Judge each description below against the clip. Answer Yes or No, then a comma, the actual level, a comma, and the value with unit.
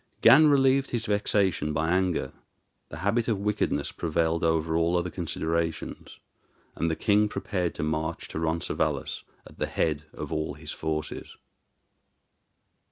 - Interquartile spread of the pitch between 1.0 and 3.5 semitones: No, average, 4.2 semitones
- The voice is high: No, very low, 85 Hz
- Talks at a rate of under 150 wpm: Yes, average, 140 wpm